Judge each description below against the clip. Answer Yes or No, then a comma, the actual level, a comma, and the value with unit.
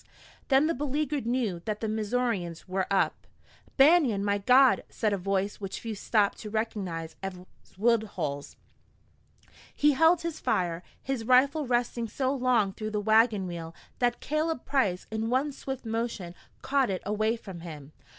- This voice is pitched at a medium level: No, high, 220 Hz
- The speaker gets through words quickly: No, average, 155 wpm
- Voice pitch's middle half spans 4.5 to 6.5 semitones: Yes, average, 5.0 semitones